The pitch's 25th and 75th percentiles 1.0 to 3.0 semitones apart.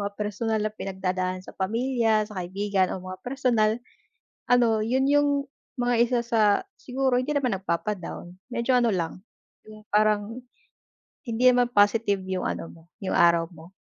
No: average, 4.3 semitones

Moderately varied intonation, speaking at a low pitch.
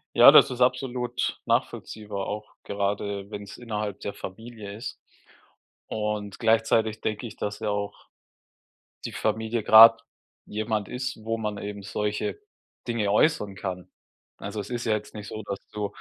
No: narrow, 1.8 semitones; low, 105 Hz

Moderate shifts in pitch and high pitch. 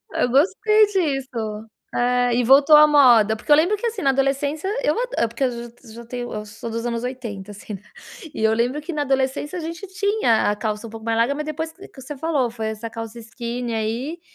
Yes: average, 4.8 semitones; very high, 250 Hz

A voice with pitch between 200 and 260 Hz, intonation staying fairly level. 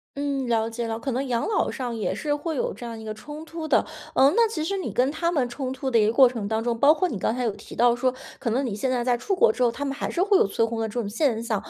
No: very high, 250 Hz; average, 4.2 semitones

